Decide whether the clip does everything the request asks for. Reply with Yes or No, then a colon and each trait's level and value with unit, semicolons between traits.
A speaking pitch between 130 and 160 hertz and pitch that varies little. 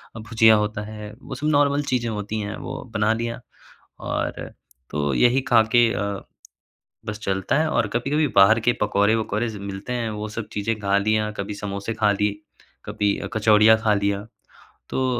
No: low, 110 Hz; narrow, 2.2 semitones